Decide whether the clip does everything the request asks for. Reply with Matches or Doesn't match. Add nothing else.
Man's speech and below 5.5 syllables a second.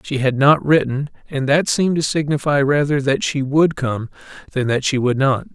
Matches